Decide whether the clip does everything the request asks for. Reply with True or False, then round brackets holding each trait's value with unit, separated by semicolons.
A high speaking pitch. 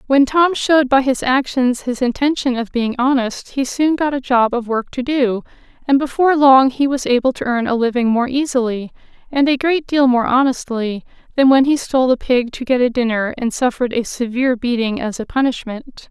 True (255 Hz)